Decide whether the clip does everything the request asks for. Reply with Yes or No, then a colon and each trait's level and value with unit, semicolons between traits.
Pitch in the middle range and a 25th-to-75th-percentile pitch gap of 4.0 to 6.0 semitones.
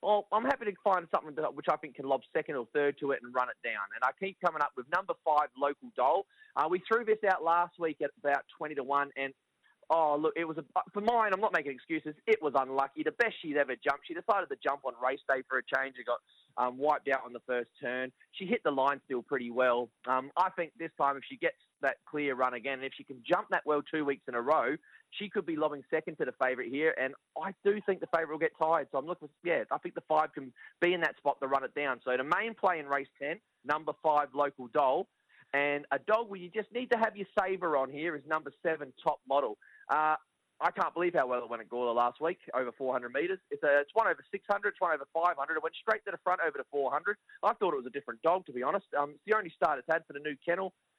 Yes: medium, 155 Hz; wide, 5.5 semitones